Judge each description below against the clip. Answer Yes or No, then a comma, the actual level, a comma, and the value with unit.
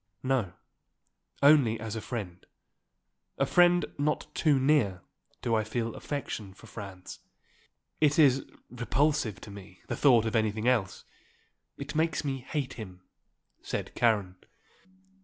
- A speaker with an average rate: No, slow, 130 wpm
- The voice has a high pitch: No, low, 120 Hz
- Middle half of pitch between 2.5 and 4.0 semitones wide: No, average, 5.3 semitones